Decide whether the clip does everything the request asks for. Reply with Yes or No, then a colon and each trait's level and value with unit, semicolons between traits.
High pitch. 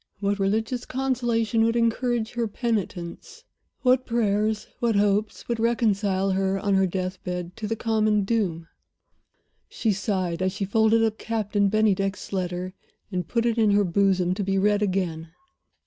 Yes: high, 205 Hz